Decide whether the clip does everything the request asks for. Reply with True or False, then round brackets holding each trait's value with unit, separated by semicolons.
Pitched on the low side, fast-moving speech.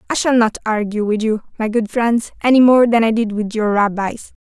False (225 Hz; 215 wpm)